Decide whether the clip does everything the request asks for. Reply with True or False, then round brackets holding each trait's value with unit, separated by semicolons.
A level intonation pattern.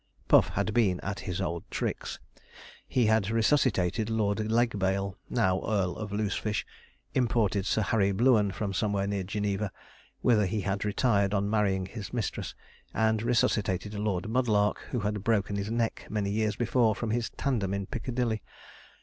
True (2.2 semitones)